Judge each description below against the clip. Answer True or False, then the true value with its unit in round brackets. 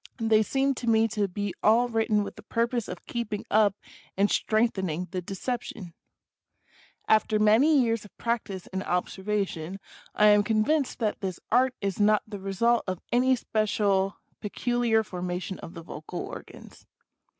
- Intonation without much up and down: False (3.2 semitones)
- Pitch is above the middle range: True (210 Hz)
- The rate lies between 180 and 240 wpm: False (160 wpm)